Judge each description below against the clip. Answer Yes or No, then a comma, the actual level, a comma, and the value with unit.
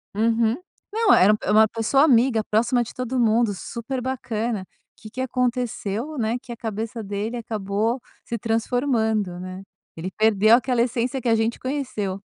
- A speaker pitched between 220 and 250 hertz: Yes, high, 230 Hz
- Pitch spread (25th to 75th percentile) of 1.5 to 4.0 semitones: Yes, narrow, 2.5 semitones